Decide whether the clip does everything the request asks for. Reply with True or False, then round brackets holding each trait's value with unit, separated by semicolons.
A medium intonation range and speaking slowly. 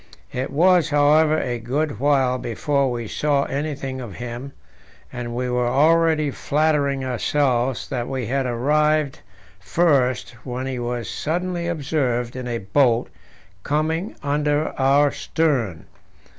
True (3.6 semitones; 130 wpm)